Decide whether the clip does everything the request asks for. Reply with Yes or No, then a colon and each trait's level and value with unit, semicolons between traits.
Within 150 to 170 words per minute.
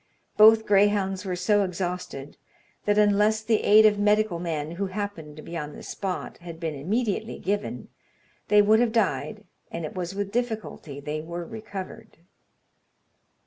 Yes: average, 155 wpm